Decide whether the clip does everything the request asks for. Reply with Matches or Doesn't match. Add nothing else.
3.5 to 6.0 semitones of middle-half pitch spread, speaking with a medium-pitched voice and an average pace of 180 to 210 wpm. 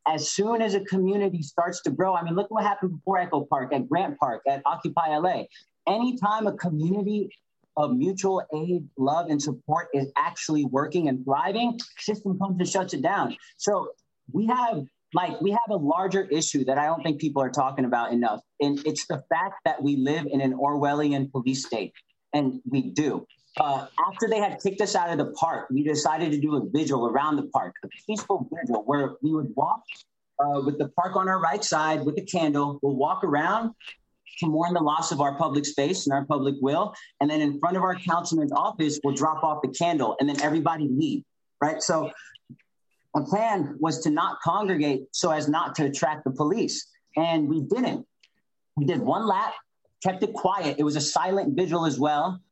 Matches